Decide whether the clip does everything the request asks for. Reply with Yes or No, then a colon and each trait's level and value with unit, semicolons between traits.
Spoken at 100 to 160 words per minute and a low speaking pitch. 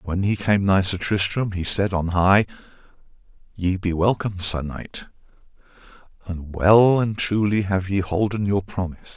Yes: average, 155 wpm; very low, 95 Hz